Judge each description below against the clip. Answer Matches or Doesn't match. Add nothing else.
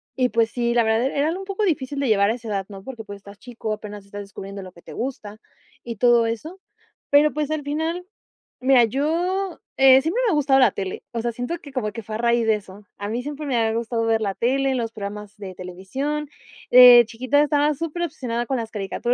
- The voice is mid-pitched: Doesn't match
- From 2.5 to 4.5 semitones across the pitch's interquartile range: Doesn't match